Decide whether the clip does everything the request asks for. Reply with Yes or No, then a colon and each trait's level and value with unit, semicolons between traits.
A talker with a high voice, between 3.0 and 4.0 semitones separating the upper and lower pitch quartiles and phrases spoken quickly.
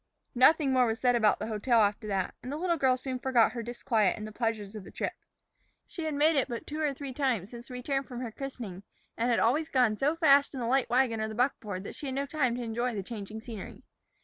Yes: high, 245 Hz; average, 3.5 semitones; fast, 255 wpm